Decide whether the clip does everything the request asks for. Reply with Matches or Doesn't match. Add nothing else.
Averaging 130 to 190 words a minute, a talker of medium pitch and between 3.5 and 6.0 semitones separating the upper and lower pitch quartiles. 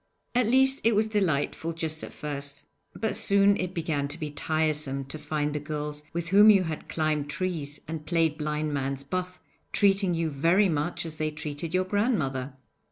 Matches